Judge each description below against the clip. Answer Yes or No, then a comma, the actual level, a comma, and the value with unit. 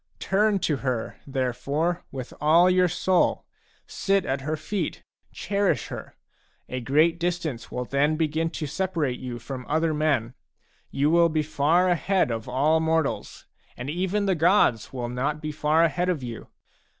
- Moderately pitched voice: Yes, medium, 155 Hz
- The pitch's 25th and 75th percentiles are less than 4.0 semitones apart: No, average, 4.6 semitones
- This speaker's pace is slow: No, average, 160 wpm